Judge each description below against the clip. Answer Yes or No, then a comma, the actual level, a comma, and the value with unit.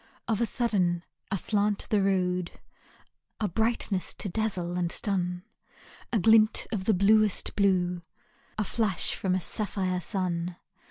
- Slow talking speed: Yes, slow, 130 wpm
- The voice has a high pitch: Yes, high, 195 Hz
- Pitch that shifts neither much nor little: Yes, average, 3.0 semitones